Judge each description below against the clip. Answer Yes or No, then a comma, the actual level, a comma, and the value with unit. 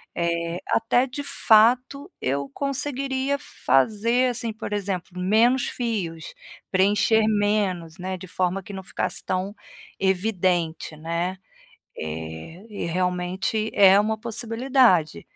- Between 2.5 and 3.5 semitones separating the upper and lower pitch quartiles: No, average, 4.6 semitones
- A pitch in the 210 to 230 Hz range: No, high, 195 Hz